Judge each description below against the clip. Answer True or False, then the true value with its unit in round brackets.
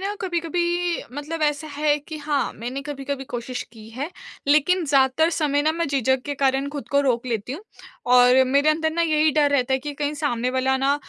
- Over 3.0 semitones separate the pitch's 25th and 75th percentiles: False (2.7 semitones)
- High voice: True (285 Hz)